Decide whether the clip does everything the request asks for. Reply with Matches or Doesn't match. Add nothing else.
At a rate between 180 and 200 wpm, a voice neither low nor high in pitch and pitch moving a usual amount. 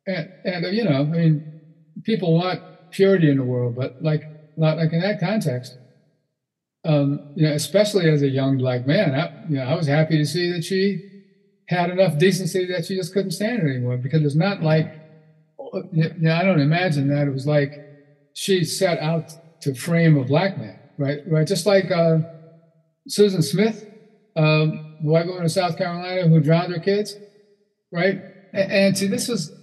Matches